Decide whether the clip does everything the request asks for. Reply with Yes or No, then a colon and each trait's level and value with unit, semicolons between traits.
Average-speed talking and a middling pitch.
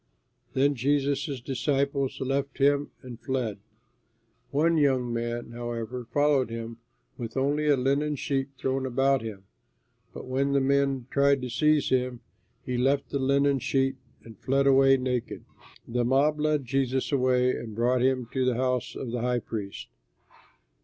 No: average, 155 wpm; low, 130 Hz